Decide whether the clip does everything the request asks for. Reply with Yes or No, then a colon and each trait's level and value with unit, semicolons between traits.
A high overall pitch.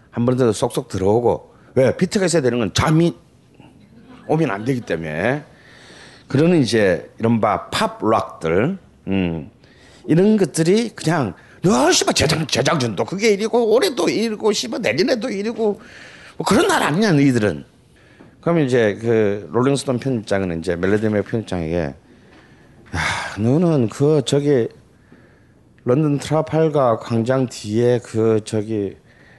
No: low, 135 Hz